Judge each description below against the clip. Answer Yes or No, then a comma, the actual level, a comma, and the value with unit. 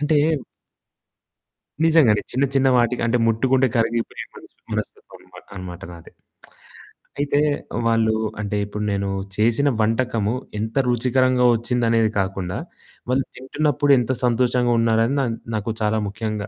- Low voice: Yes, low, 115 Hz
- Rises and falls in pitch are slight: No, average, 3.1 semitones